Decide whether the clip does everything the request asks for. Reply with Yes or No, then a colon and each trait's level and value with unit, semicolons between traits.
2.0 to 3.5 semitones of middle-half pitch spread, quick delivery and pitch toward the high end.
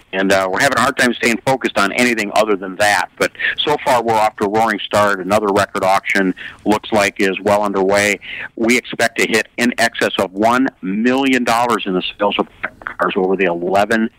No: average, 2.9 semitones; fast, 210 wpm; low, 105 Hz